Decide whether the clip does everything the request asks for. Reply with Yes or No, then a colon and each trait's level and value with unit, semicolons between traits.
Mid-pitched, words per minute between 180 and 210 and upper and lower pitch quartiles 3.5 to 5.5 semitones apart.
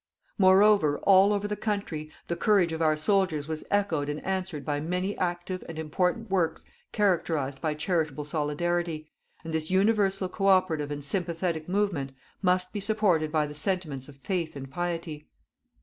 No: medium, 175 Hz; average, 160 wpm; average, 3.9 semitones